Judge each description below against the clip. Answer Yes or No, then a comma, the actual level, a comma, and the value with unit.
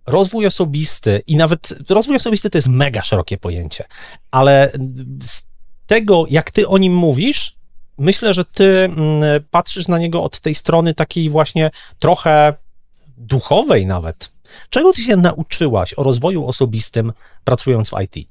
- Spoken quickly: No, average, 140 wpm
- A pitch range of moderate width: No, wide, 5.8 semitones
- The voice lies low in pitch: No, medium, 155 Hz